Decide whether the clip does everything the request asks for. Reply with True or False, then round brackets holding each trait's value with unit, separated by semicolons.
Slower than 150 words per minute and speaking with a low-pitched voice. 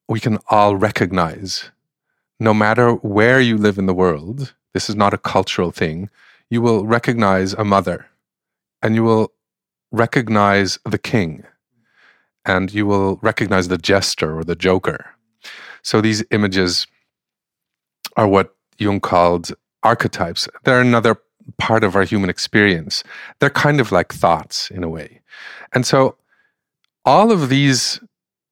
True (140 wpm; 105 Hz)